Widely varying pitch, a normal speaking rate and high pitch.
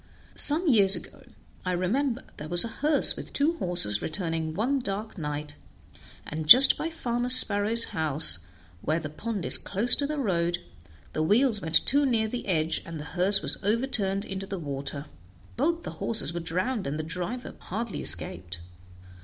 Yes: wide, 7.0 semitones; average, 170 wpm; high, 195 Hz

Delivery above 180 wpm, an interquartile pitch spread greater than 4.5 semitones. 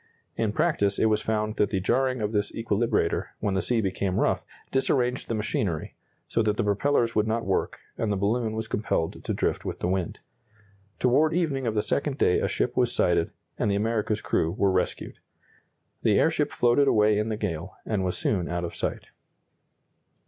No: average, 190 wpm; average, 3.0 semitones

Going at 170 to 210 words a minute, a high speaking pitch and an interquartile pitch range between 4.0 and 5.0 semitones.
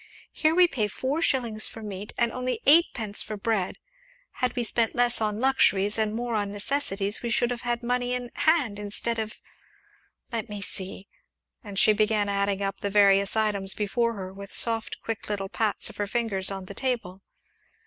No: average, 185 wpm; high, 215 Hz; average, 3.2 semitones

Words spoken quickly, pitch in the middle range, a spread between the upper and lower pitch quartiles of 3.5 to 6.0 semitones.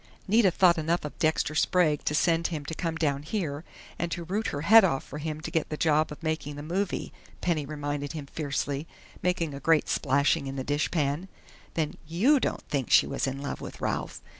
No: fast, 215 wpm; medium, 155 Hz; average, 2.8 semitones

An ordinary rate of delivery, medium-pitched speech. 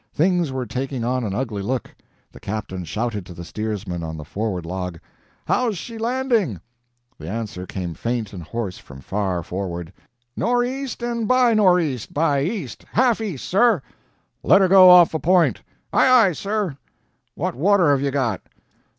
No: average, 170 wpm; low, 130 Hz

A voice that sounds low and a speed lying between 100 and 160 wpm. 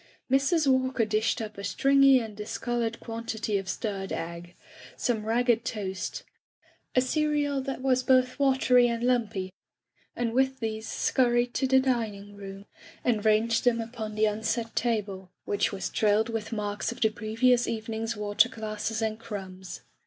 No: high, 225 Hz; average, 155 wpm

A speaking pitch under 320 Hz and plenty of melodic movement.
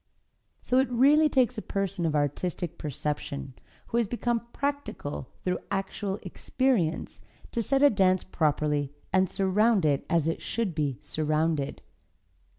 Yes: medium, 185 Hz; wide, 7.4 semitones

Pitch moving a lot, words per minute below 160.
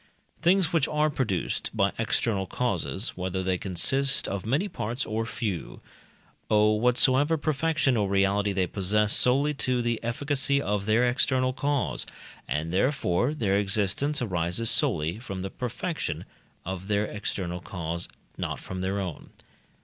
Yes: wide, 5.8 semitones; average, 140 wpm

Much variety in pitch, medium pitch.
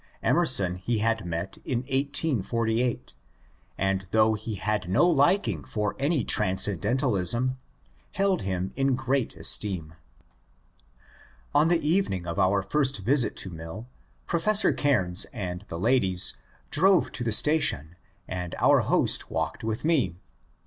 No: wide, 6.8 semitones; low, 115 Hz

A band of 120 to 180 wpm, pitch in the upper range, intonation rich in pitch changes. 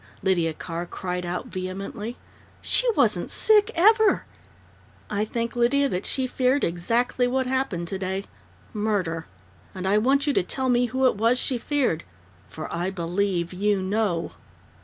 Yes: average, 155 wpm; high, 210 Hz; wide, 6.0 semitones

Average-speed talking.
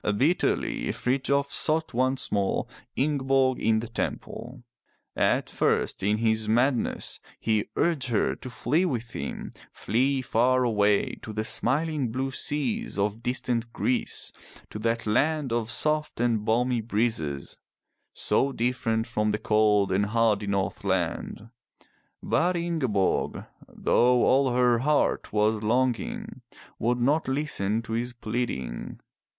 No: slow, 130 wpm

